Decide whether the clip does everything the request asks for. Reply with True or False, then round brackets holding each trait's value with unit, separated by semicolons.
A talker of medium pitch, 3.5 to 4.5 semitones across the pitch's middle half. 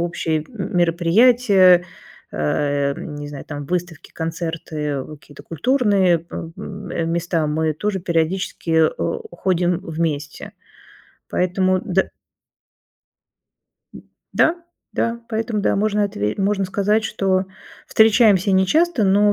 True (180 Hz; 4.0 semitones)